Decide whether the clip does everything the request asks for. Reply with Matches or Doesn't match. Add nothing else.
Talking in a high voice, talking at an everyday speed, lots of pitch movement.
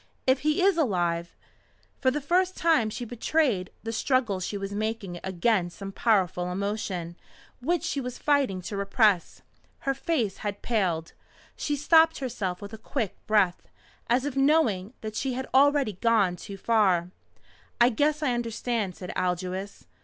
Matches